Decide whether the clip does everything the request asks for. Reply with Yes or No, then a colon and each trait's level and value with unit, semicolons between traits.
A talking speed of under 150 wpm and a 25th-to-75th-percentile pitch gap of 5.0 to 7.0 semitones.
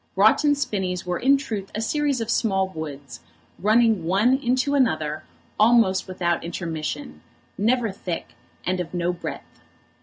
Yes: average, 140 wpm; wide, 5.6 semitones